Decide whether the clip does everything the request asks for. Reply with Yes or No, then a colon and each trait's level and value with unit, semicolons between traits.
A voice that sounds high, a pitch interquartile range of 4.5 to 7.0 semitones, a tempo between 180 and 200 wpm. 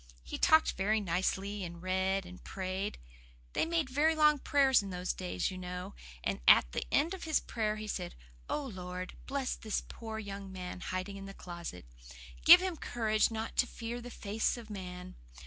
Yes: high, 200 Hz; average, 4.9 semitones; average, 185 wpm